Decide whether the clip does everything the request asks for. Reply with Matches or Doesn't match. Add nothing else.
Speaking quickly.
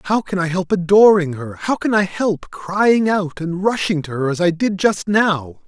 Matches